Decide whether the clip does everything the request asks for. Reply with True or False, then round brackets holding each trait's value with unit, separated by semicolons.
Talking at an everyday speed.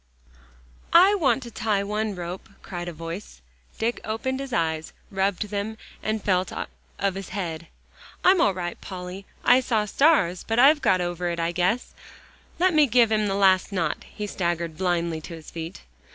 True (175 wpm)